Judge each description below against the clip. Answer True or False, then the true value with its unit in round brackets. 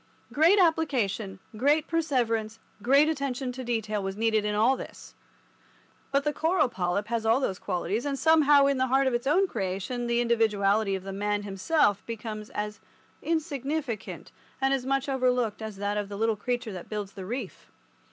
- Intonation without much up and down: False (4.9 semitones)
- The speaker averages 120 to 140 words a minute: False (175 wpm)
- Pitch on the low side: False (235 Hz)